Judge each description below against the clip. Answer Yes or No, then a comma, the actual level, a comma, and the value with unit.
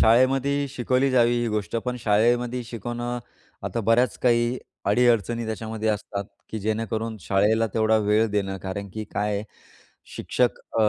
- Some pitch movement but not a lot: No, narrow, 2.2 semitones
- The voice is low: Yes, low, 115 Hz